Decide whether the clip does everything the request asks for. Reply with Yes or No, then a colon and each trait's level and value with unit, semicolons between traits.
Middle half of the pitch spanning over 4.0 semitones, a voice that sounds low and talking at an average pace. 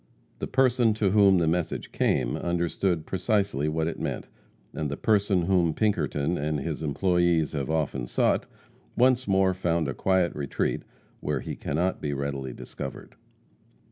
Yes: average, 4.5 semitones; very low, 85 Hz; average, 150 wpm